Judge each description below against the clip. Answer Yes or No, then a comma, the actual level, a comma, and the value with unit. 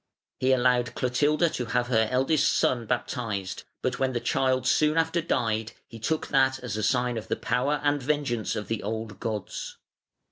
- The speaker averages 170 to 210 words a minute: Yes, average, 180 wpm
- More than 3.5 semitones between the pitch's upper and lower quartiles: No, average, 3.2 semitones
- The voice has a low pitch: Yes, low, 125 Hz